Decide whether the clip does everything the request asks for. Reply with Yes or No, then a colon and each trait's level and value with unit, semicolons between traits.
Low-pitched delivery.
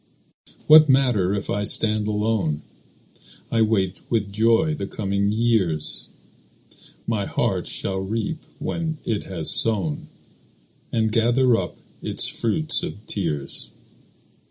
Yes: low, 110 Hz